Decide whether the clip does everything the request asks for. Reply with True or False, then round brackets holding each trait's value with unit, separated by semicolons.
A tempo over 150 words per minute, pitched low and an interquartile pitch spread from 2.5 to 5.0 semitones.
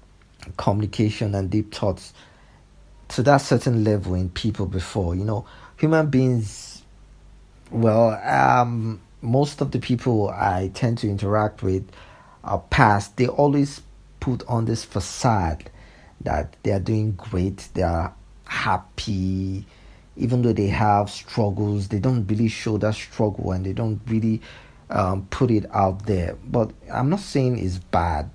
False (145 wpm; 105 Hz; 3.5 semitones)